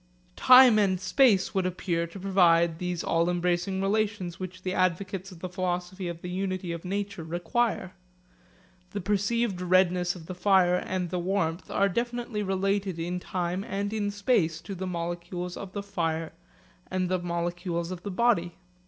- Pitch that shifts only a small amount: Yes, narrow, 2.2 semitones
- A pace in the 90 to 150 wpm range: No, average, 165 wpm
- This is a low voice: No, medium, 185 Hz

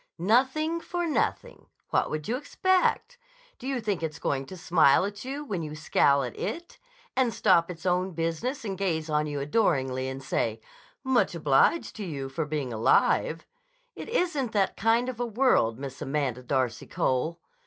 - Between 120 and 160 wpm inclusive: No, average, 175 wpm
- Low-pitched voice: No, medium, 170 Hz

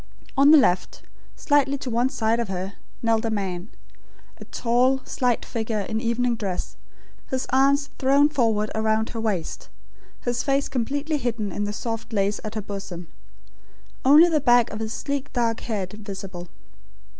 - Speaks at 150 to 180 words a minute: Yes, average, 160 wpm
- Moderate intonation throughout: Yes, average, 4.0 semitones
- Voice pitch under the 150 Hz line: No, high, 230 Hz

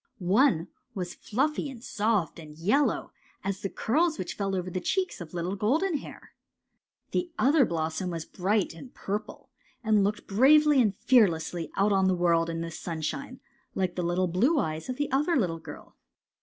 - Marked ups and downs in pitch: Yes, wide, 6.9 semitones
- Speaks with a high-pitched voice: Yes, high, 195 Hz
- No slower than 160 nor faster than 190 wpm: Yes, average, 170 wpm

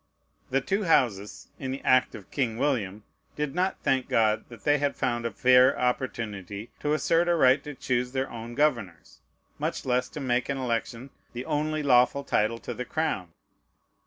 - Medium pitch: No, low, 125 Hz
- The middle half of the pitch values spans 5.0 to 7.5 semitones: No, average, 3.6 semitones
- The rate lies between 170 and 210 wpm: Yes, average, 180 wpm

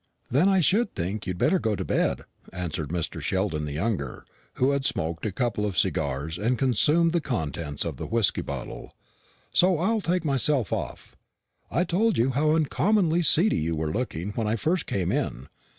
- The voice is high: No, low, 115 Hz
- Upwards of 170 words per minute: Yes, average, 180 wpm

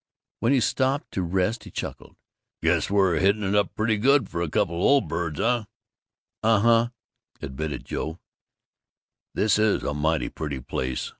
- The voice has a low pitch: Yes, low, 100 Hz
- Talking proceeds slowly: No, average, 165 wpm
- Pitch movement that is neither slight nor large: No, wide, 5.8 semitones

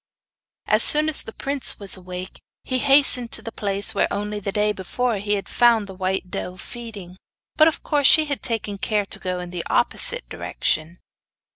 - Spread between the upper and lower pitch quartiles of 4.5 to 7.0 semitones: Yes, average, 4.8 semitones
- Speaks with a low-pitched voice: No, high, 210 Hz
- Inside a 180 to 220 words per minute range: Yes, average, 190 wpm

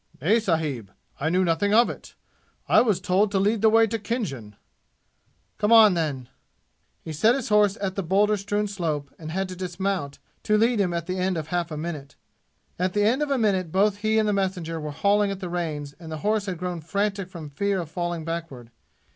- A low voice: No, medium, 185 Hz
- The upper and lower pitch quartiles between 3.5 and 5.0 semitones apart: Yes, average, 4.2 semitones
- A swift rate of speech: Yes, fast, 215 wpm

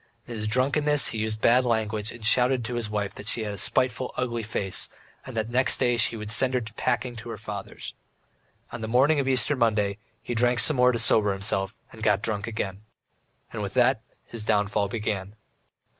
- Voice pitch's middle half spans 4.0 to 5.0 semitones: No, average, 2.9 semitones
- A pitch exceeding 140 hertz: No, low, 115 Hz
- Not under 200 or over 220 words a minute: Yes, fast, 205 wpm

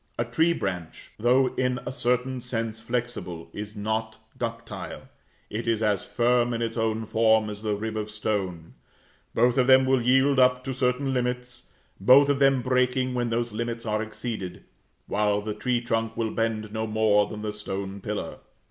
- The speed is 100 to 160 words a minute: No, average, 175 wpm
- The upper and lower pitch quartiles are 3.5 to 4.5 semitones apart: No, average, 2.7 semitones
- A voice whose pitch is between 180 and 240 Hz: No, low, 115 Hz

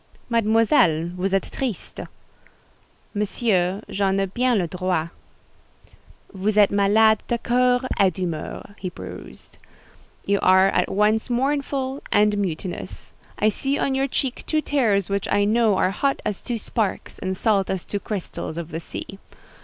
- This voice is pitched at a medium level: No, high, 205 Hz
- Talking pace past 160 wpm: No, average, 150 wpm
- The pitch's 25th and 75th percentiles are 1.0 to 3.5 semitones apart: No, average, 3.9 semitones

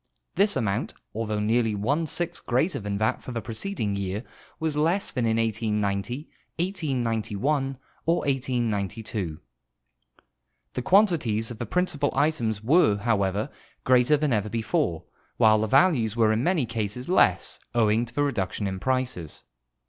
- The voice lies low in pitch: Yes, low, 115 Hz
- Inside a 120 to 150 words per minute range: Yes, average, 145 wpm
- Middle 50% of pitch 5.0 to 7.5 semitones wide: Yes, wide, 5.4 semitones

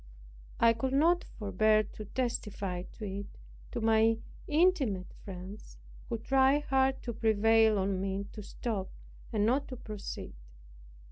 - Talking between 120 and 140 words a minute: Yes, slow, 135 wpm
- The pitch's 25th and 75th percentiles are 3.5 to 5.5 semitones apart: Yes, average, 4.4 semitones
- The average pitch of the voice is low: No, high, 220 Hz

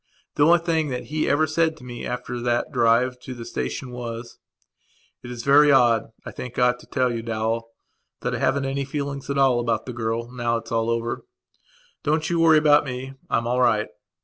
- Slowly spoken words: No, fast, 205 wpm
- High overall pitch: No, low, 125 Hz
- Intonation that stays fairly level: No, average, 3.2 semitones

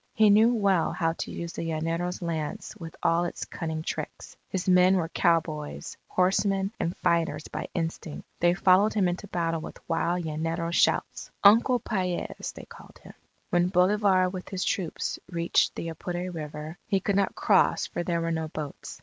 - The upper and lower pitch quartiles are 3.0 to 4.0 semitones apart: No, narrow, 2.4 semitones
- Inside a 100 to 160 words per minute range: No, average, 175 wpm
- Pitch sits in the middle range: Yes, medium, 175 Hz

